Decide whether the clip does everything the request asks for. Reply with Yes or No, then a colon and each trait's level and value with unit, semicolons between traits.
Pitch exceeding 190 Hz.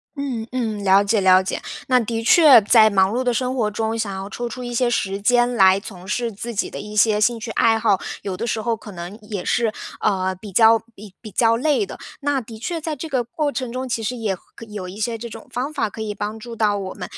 Yes: high, 225 Hz